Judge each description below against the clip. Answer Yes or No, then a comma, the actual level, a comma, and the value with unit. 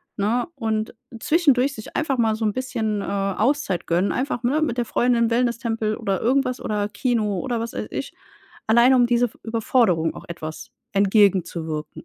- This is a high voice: Yes, high, 225 Hz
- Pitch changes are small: No, average, 3.5 semitones